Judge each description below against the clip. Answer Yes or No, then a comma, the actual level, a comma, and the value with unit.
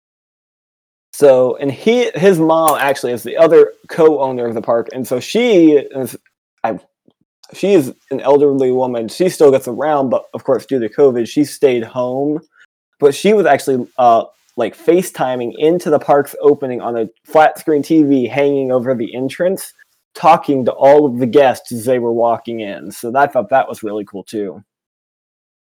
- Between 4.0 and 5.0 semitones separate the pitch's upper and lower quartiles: Yes, average, 4.5 semitones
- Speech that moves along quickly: No, average, 175 wpm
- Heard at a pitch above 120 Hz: Yes, low, 135 Hz